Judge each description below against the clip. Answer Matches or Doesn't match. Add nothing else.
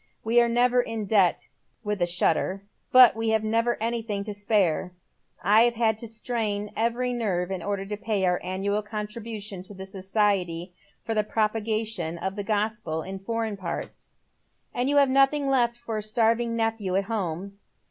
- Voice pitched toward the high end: Matches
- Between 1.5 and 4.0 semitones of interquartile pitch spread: Matches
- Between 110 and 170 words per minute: Doesn't match